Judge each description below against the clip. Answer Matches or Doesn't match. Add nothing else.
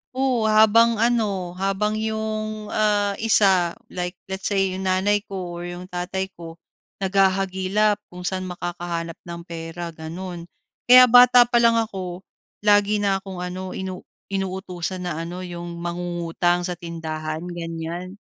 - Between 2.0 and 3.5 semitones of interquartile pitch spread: Matches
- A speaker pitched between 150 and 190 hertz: Matches